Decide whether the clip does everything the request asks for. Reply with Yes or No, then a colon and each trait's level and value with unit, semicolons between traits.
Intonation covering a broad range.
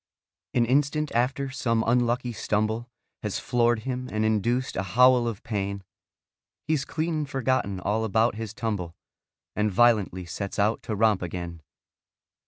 No: average, 3.6 semitones